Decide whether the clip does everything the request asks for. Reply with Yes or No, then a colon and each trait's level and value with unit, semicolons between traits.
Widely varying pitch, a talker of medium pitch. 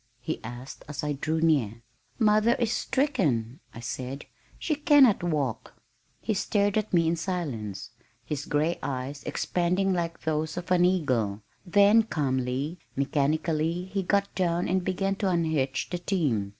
Yes: wide, 5.8 semitones; medium, 165 Hz